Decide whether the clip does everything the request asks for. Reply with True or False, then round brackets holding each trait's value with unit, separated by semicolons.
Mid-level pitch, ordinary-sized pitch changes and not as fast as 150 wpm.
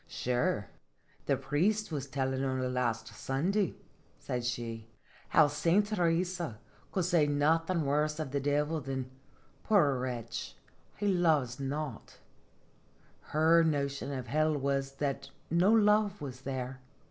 True (145 Hz; 4.1 semitones; 140 wpm)